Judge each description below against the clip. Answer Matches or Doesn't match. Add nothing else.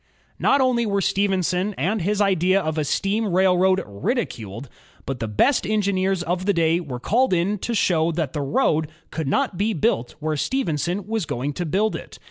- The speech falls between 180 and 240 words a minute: Matches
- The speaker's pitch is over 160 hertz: Matches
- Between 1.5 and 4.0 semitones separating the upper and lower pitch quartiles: Doesn't match